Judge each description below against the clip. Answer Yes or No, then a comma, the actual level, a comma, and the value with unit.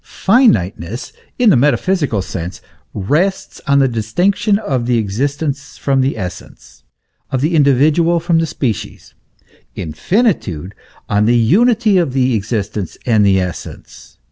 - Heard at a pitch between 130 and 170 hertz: Yes, low, 135 Hz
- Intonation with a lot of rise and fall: Yes, wide, 8.2 semitones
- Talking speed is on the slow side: Yes, slow, 120 wpm